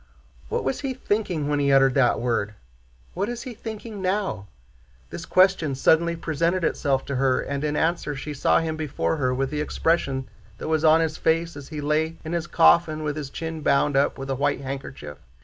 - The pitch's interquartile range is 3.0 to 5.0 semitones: Yes, average, 3.6 semitones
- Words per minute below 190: No, average, 200 wpm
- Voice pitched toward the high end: No, medium, 155 Hz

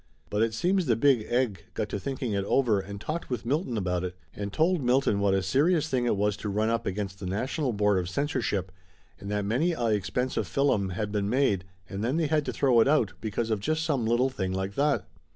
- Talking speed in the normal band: No, fast, 240 wpm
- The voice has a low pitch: Yes, low, 115 Hz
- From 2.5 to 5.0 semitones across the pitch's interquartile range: No, wide, 5.4 semitones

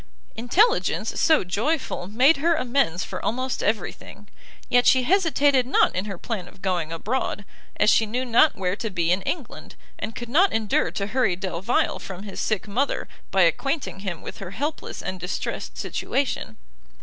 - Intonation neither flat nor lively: No, wide, 6.0 semitones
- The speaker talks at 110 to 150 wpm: No, average, 175 wpm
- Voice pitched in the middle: No, high, 220 Hz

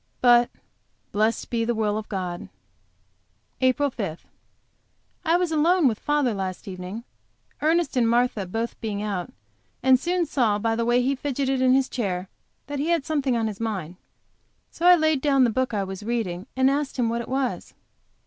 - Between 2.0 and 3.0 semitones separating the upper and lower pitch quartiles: No, average, 4.7 semitones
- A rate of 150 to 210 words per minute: Yes, average, 180 wpm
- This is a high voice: Yes, high, 240 Hz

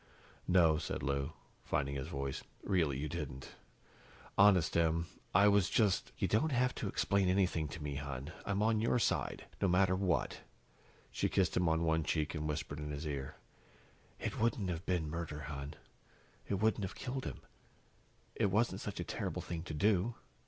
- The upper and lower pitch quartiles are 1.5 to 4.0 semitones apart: No, average, 4.9 semitones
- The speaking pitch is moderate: No, very low, 85 Hz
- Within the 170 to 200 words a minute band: Yes, average, 180 wpm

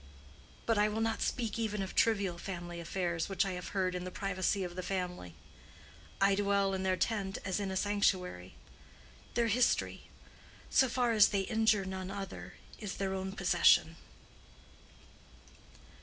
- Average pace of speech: Yes, average, 155 wpm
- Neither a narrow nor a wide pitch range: No, narrow, 2.3 semitones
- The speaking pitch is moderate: No, high, 195 Hz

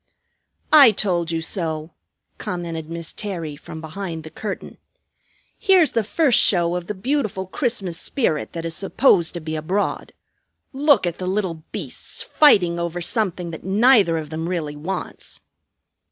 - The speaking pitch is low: No, medium, 175 Hz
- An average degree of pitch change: Yes, average, 4.3 semitones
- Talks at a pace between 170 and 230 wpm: No, average, 150 wpm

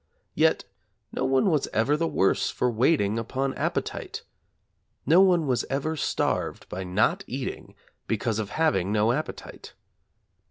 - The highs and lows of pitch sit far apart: Yes, wide, 6.1 semitones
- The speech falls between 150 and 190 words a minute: No, slow, 135 wpm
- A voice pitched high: No, low, 135 Hz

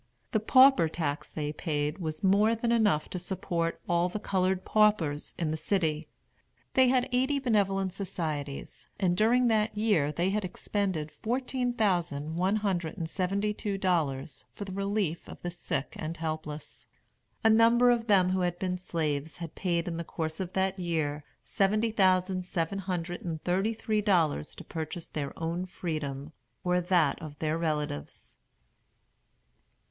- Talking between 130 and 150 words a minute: No, average, 165 wpm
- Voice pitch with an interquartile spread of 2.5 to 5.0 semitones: Yes, average, 4.3 semitones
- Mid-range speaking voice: Yes, medium, 180 Hz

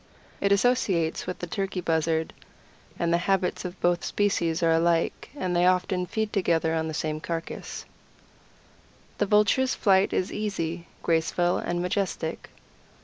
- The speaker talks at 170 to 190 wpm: No, average, 145 wpm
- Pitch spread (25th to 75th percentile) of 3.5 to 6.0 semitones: No, average, 2.9 semitones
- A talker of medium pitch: Yes, medium, 175 Hz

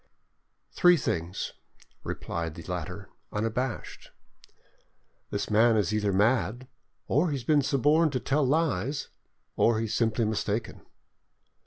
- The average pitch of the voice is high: No, low, 115 Hz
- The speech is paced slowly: Yes, slow, 125 wpm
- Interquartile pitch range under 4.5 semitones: No, average, 4.8 semitones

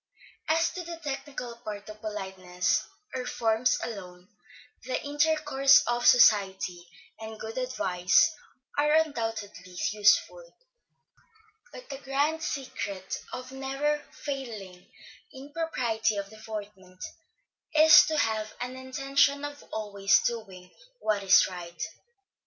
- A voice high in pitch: Yes, high, 230 Hz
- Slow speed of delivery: Yes, slow, 110 wpm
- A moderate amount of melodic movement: No, wide, 5.8 semitones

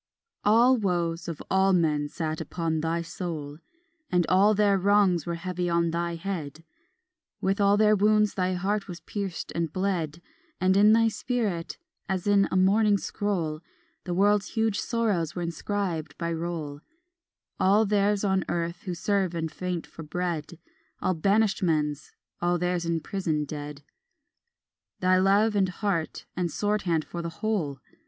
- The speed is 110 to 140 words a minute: No, average, 160 wpm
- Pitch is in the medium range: Yes, medium, 180 Hz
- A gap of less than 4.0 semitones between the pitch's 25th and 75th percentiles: Yes, average, 3.3 semitones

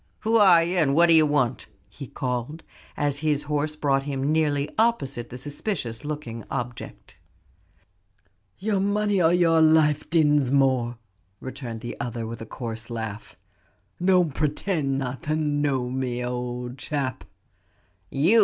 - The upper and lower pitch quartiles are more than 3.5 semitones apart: Yes, average, 4.3 semitones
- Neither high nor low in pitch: Yes, medium, 145 Hz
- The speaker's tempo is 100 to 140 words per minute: Yes, slow, 135 wpm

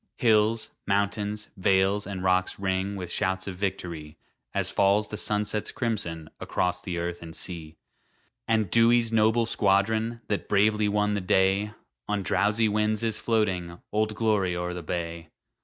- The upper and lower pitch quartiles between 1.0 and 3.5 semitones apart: Yes, average, 2.8 semitones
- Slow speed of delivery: No, average, 150 wpm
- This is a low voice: Yes, low, 100 Hz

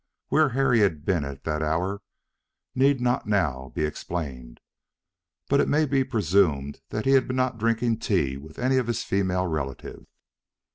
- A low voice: Yes, low, 100 Hz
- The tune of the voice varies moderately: No, wide, 8.4 semitones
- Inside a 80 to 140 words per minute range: No, average, 165 wpm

